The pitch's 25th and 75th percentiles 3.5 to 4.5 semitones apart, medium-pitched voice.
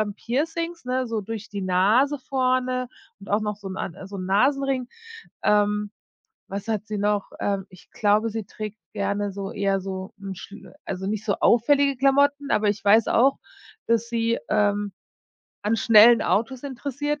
No: average, 4.1 semitones; high, 215 Hz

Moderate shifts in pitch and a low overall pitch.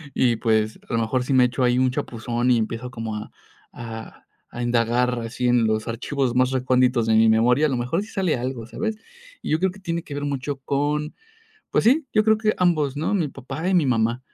Yes: average, 4.2 semitones; low, 125 Hz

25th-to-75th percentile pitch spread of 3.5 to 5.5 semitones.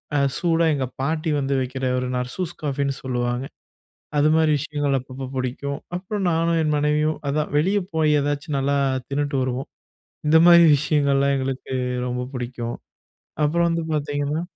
No: average, 2.8 semitones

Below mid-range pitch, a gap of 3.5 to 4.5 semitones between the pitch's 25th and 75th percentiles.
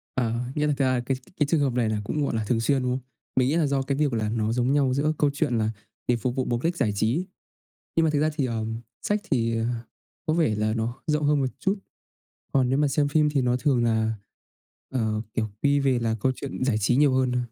Yes: low, 130 Hz; average, 3.8 semitones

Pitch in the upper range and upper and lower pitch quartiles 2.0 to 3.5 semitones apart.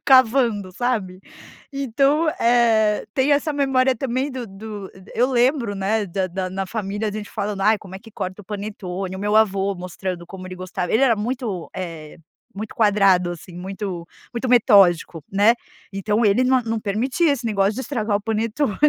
No: high, 210 Hz; average, 4.0 semitones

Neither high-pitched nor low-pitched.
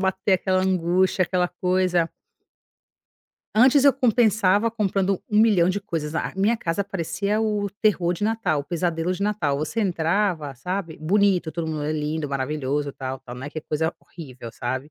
Yes: medium, 180 Hz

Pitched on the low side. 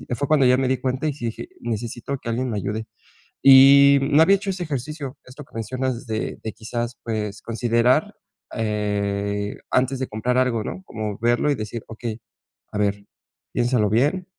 Yes: low, 120 Hz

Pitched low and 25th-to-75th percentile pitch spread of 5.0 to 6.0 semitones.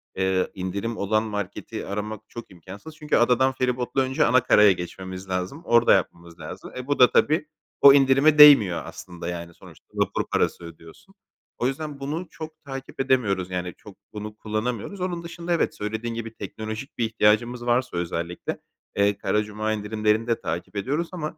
Yes: low, 110 Hz; wide, 5.6 semitones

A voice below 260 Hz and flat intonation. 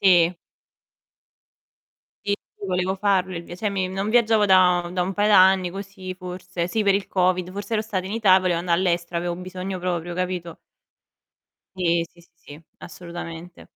Yes: medium, 185 Hz; narrow, 1.8 semitones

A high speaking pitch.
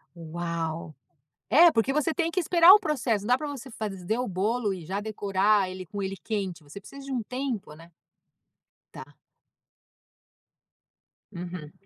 Yes: high, 205 Hz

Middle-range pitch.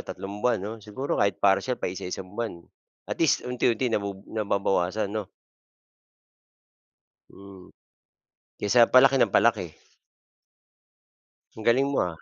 No: low, 105 Hz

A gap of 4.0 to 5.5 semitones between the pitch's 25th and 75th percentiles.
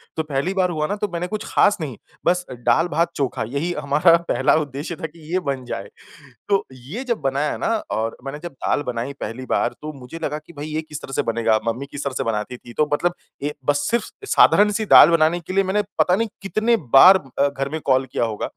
Yes: average, 4.7 semitones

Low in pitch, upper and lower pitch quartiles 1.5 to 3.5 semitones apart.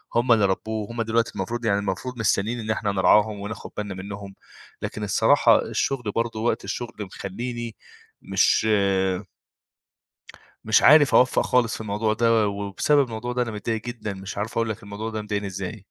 Yes: low, 110 Hz; narrow, 2.5 semitones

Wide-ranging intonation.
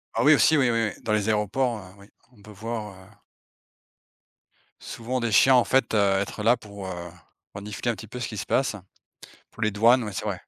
No: average, 2.9 semitones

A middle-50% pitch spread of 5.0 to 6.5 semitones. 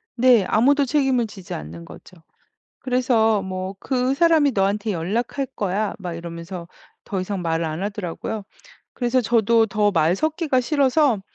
Yes: wide, 5.6 semitones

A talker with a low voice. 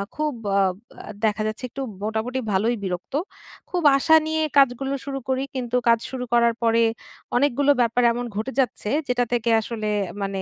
No: high, 240 Hz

